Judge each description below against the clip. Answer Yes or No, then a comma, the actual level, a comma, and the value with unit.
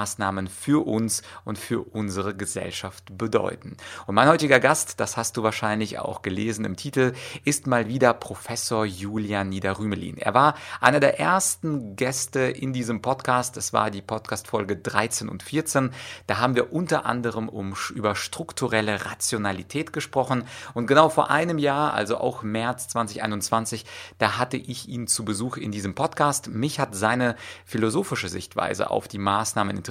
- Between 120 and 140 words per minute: No, average, 155 wpm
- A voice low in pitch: Yes, low, 115 Hz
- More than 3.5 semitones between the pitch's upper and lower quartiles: Yes, average, 3.9 semitones